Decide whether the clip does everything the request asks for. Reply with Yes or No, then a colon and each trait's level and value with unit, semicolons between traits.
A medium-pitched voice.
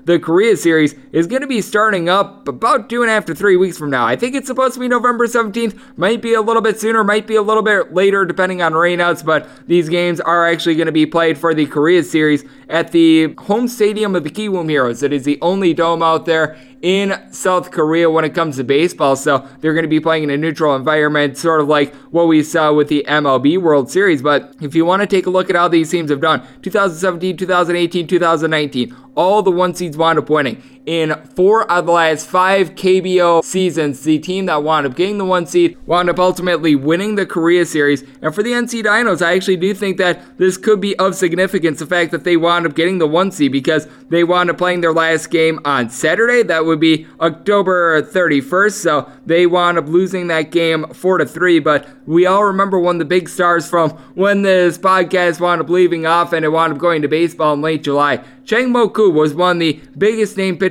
Yes: medium, 170 Hz